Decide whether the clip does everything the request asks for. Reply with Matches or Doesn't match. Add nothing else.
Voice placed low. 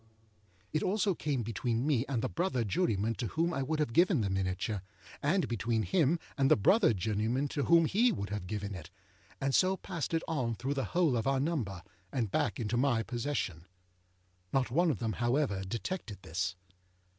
Matches